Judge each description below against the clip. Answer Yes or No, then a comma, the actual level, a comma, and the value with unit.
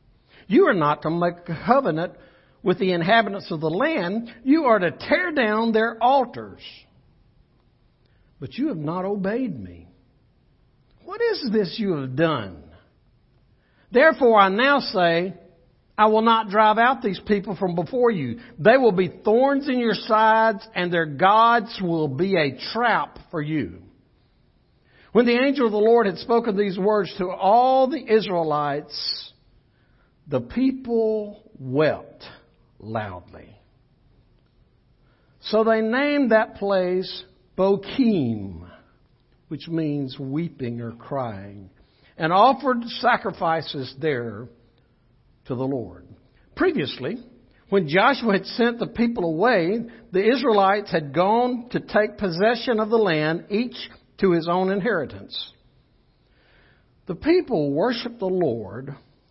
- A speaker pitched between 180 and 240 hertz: Yes, high, 190 Hz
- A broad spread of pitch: Yes, wide, 7.9 semitones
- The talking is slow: Yes, slow, 125 wpm